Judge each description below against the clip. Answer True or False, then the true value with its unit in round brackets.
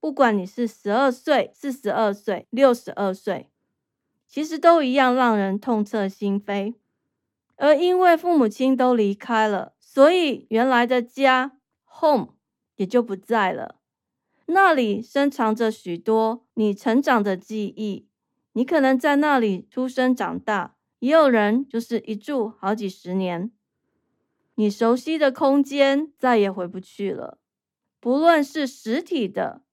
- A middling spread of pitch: True (4.8 semitones)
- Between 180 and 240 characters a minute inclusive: True (210 characters per minute)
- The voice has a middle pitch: False (240 Hz)